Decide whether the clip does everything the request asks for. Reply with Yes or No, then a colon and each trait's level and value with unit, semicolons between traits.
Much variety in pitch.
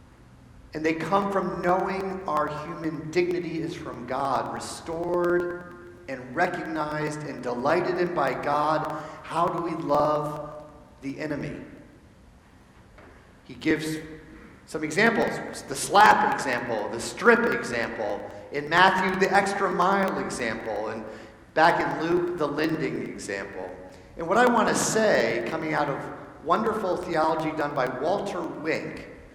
No: average, 3.3 semitones